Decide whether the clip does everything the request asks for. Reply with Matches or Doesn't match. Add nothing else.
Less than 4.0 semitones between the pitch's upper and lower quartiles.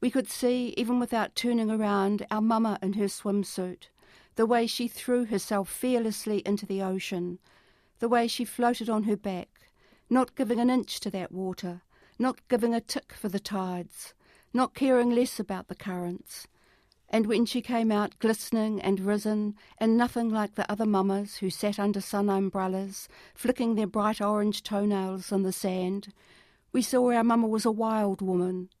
Matches